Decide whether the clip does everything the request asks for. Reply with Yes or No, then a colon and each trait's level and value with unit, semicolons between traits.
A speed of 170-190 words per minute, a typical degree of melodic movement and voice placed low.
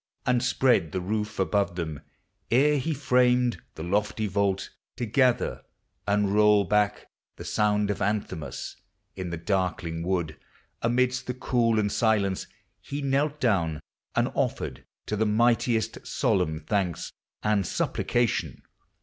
No: slow, 135 wpm; average, 4.4 semitones; low, 105 Hz